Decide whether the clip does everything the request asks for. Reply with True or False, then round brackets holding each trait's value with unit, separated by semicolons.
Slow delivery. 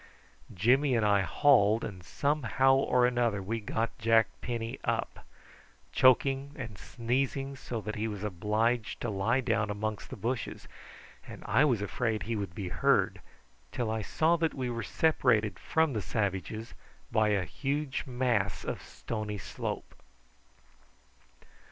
False (145 wpm)